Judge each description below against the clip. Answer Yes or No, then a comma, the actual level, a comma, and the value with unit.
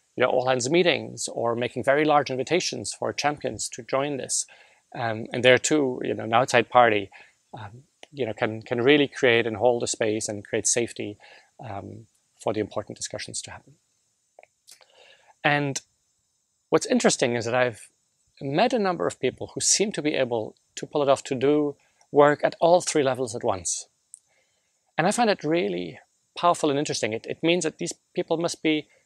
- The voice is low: Yes, low, 130 Hz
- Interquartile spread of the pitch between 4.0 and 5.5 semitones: Yes, average, 4.5 semitones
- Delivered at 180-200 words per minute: Yes, average, 185 wpm